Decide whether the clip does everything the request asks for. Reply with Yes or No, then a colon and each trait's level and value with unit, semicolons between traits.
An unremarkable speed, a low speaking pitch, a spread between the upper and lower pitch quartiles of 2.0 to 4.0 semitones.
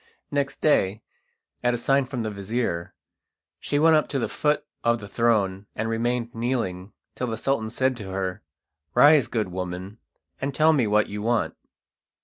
No: average, 170 wpm; low, 115 Hz; average, 4.6 semitones